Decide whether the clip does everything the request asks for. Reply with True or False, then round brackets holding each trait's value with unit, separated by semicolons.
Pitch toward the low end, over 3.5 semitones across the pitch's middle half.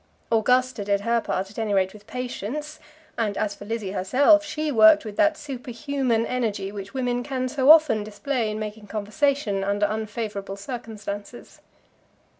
False (220 Hz; 3.9 semitones)